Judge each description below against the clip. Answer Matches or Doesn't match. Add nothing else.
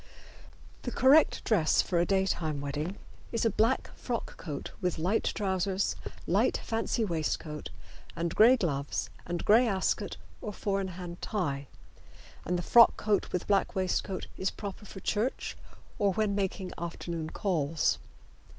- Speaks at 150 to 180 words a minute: Doesn't match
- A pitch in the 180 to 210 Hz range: Matches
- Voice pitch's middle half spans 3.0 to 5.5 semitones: Matches